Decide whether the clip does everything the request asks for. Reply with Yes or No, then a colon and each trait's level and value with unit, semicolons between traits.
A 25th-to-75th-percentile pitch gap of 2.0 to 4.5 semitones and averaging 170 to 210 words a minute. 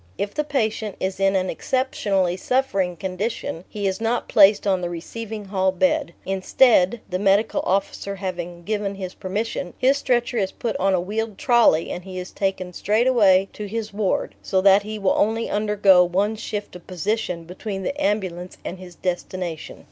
Yes: average, 3.0 semitones; average, 180 wpm